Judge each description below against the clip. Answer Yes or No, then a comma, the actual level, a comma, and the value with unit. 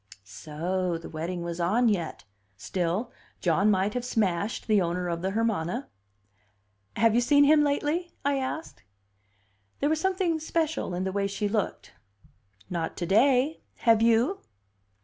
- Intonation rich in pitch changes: Yes, wide, 7.5 semitones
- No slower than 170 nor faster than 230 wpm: No, average, 150 wpm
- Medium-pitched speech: No, high, 210 Hz